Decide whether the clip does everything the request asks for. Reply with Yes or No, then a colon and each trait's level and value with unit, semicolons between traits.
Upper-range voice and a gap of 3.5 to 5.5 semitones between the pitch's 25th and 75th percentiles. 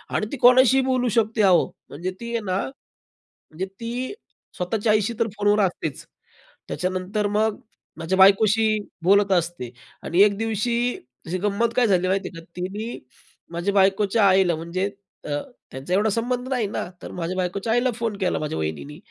Yes: high, 200 Hz; average, 3.8 semitones